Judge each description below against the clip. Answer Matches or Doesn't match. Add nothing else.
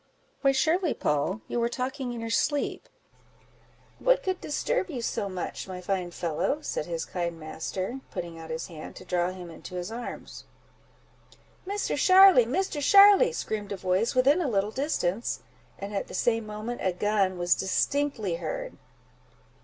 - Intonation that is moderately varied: Doesn't match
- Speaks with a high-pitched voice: Matches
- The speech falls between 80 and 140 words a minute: Doesn't match